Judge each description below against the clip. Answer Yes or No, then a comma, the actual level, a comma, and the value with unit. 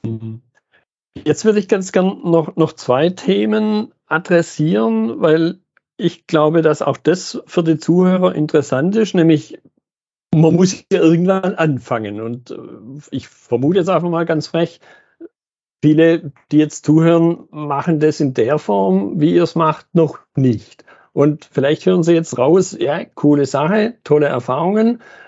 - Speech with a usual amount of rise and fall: Yes, average, 3.6 semitones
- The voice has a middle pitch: Yes, medium, 160 Hz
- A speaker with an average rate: Yes, average, 145 wpm